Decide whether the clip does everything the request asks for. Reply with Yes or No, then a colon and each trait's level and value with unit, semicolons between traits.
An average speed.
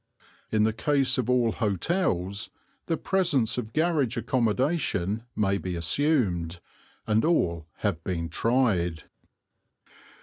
No: slow, 110 wpm